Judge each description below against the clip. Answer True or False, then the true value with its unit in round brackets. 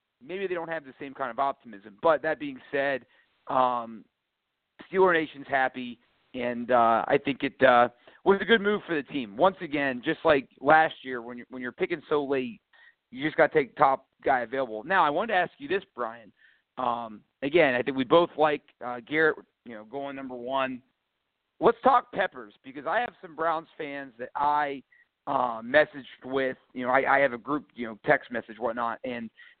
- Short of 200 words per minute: False (205 wpm)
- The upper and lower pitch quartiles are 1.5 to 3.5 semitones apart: False (4.0 semitones)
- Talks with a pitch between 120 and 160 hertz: True (140 Hz)